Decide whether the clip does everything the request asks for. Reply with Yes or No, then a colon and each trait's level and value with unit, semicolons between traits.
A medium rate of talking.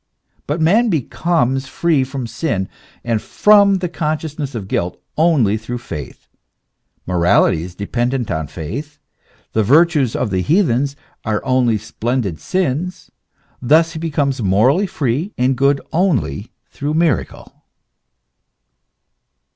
No: slow, 125 wpm